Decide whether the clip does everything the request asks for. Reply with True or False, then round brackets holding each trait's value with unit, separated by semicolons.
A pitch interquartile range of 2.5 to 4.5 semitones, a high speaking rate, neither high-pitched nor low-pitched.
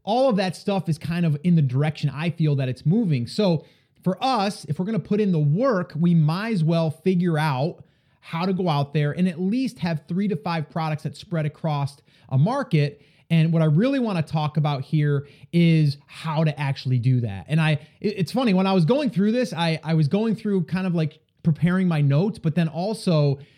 True (3.8 semitones; 225 wpm; 165 Hz)